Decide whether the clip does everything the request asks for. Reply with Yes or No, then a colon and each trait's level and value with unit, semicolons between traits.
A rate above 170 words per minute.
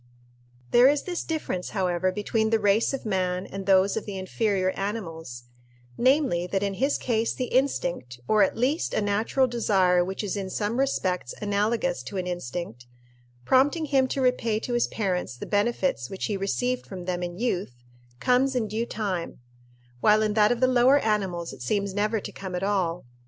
Yes: average, 185 wpm